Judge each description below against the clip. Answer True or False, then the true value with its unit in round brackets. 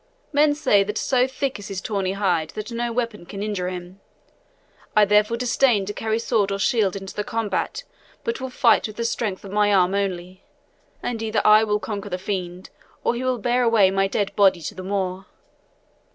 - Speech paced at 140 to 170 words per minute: False (200 wpm)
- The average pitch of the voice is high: True (205 Hz)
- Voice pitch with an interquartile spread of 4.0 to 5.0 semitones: False (3.1 semitones)